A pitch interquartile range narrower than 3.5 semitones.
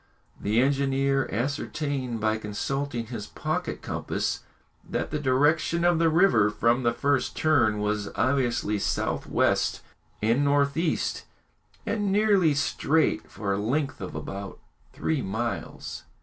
No: average, 5.2 semitones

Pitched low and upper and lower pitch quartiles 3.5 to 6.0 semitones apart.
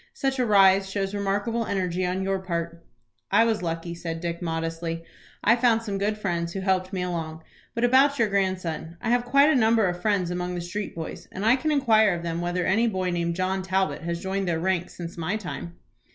No: high, 190 Hz; average, 3.8 semitones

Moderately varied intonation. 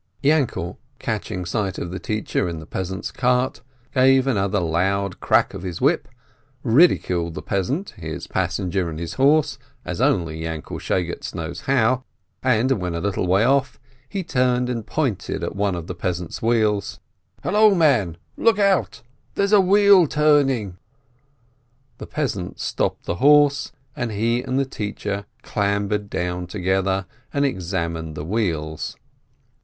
No: wide, 6.8 semitones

